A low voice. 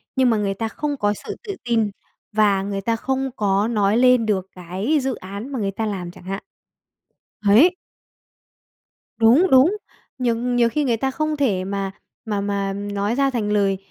No: high, 220 Hz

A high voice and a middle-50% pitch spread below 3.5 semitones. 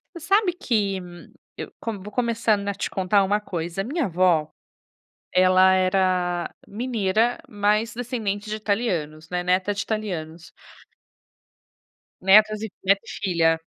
Yes: high, 200 Hz; average, 3.0 semitones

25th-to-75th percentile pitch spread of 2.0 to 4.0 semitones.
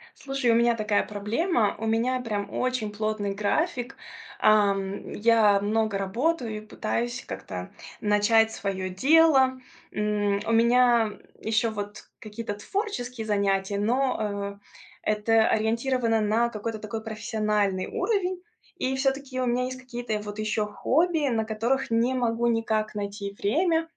Yes: average, 3.3 semitones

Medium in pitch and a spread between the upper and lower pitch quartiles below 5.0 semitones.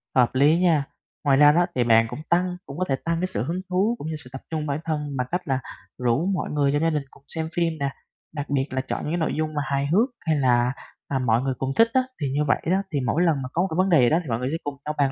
Yes: medium, 150 Hz; average, 3.9 semitones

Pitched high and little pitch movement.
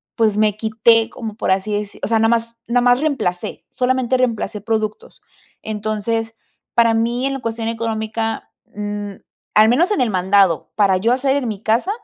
Yes: high, 225 Hz; narrow, 2.1 semitones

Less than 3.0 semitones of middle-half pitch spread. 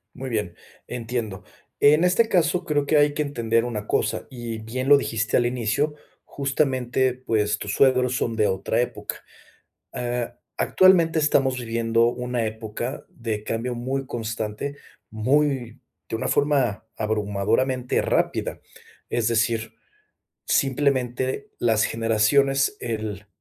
No: average, 3.5 semitones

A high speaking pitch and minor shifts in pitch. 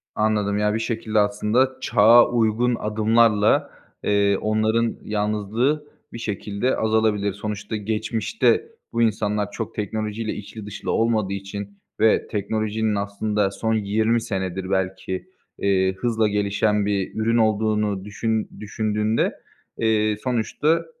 No: low, 105 Hz; narrow, 1.6 semitones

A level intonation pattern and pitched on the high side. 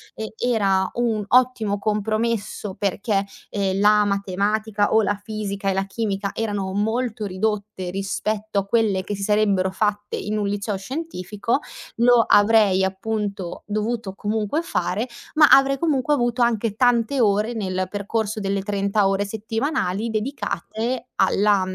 Yes: narrow, 2.3 semitones; high, 210 Hz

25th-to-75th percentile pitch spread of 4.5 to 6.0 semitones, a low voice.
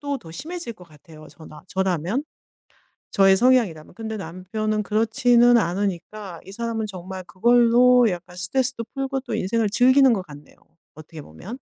No: average, 5.2 semitones; high, 215 Hz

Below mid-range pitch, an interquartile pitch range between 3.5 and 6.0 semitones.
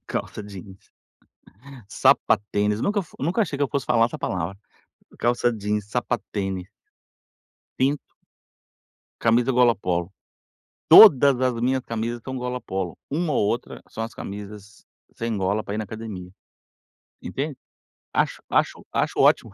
Yes: low, 115 Hz; average, 4.0 semitones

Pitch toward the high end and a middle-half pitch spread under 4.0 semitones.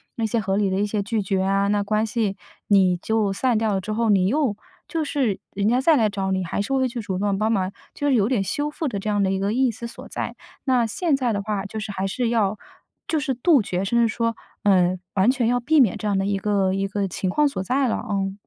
Yes: high, 210 Hz; average, 3.6 semitones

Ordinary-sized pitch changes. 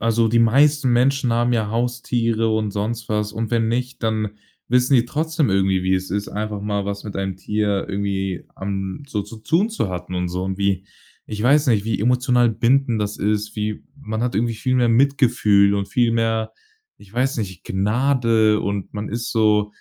Yes: average, 3.1 semitones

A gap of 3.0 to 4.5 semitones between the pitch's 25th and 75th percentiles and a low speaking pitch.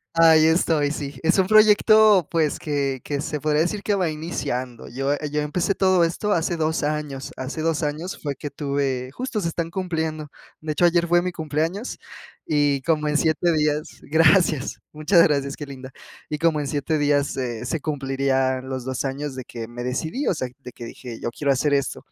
No: average, 3.3 semitones; medium, 150 Hz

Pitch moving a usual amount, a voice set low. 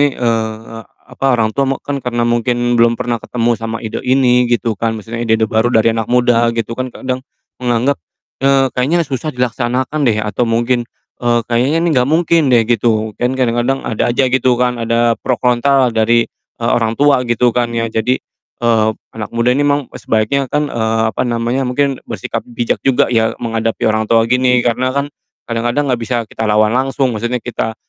No: narrow, 2.0 semitones; low, 120 Hz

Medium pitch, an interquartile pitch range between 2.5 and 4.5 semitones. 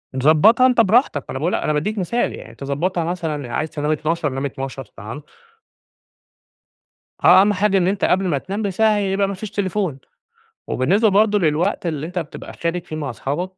No: medium, 175 Hz; average, 5.3 semitones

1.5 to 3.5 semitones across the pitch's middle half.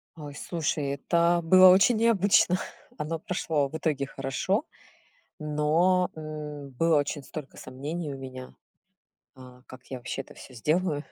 No: average, 3.9 semitones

